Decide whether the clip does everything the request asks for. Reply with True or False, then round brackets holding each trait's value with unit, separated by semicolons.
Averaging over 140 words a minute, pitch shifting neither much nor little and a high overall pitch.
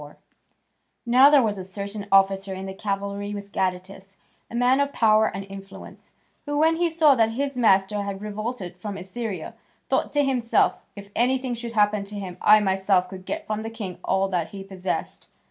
True (190 wpm; 3.5 semitones; 205 Hz)